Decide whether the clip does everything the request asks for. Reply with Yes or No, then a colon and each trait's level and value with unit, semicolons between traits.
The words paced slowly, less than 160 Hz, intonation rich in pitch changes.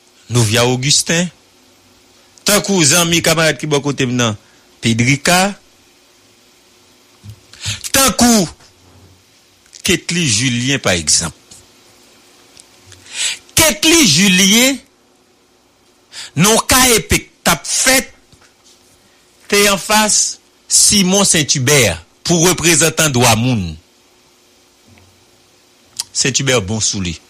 Yes: slow, 75 wpm; medium, 140 Hz; wide, 9.0 semitones